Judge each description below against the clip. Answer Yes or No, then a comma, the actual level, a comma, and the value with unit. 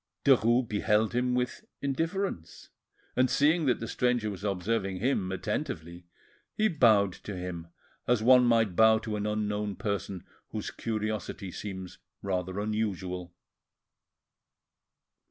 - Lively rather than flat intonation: No, average, 4.3 semitones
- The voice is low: Yes, low, 105 Hz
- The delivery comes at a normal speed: No, slow, 120 wpm